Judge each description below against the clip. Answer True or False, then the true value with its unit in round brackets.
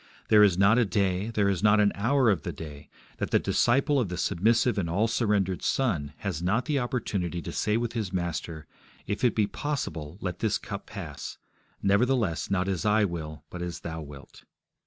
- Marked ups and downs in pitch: False (4.5 semitones)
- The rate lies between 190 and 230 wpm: True (200 wpm)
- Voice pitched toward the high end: False (100 Hz)